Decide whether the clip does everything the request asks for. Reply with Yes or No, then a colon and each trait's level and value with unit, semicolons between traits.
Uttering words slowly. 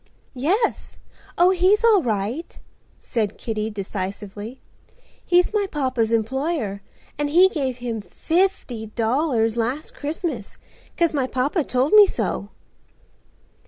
Yes: slow, 115 wpm